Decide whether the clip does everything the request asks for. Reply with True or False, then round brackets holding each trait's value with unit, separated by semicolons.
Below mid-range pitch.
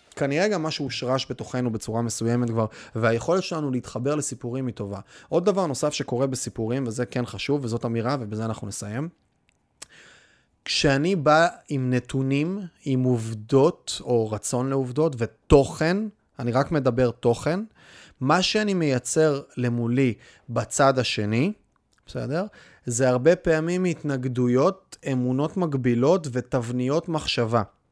True (130 Hz)